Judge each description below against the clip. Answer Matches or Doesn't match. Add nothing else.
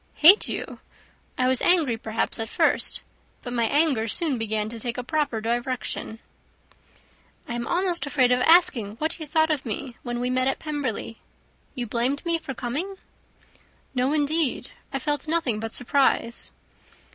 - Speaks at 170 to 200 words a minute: Doesn't match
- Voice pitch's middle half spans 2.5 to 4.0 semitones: Doesn't match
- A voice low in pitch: Doesn't match